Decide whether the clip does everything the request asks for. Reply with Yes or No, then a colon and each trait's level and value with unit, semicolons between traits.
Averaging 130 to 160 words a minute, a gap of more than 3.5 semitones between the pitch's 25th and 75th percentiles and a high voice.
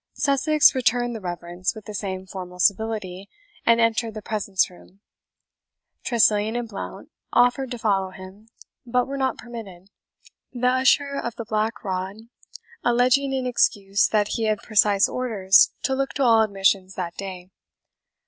Yes: average, 150 wpm; average, 4.1 semitones; high, 220 Hz